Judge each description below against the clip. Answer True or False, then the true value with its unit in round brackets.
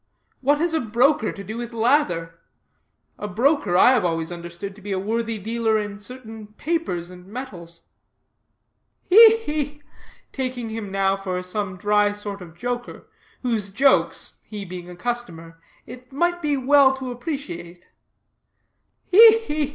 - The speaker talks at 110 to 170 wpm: True (150 wpm)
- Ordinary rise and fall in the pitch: False (6.1 semitones)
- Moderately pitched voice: False (220 Hz)